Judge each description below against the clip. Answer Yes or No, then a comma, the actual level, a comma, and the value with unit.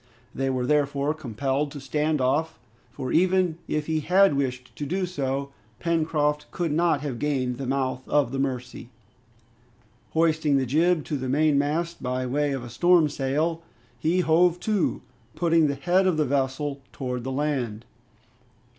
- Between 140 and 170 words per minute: Yes, average, 160 wpm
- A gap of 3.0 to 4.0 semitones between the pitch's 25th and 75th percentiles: Yes, average, 3.4 semitones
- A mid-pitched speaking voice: Yes, medium, 145 Hz